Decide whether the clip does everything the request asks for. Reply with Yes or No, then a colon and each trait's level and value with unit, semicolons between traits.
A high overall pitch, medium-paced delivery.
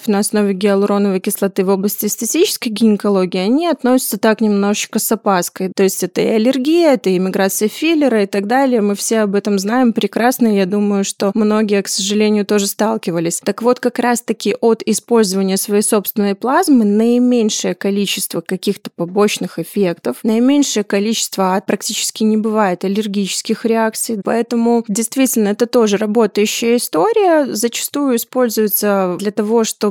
Yes: high, 215 Hz; average, 145 wpm